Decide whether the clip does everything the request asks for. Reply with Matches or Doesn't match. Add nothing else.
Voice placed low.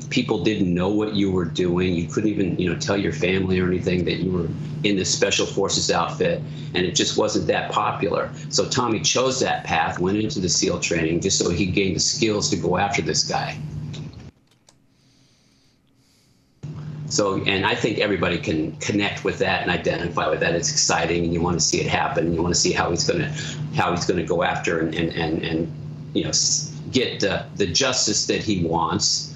Matches